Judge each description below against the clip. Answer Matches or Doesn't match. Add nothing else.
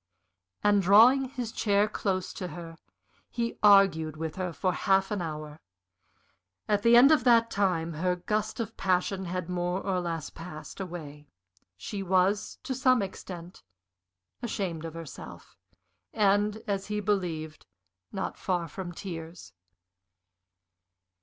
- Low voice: Doesn't match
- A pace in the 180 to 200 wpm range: Doesn't match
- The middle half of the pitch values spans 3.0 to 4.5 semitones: Matches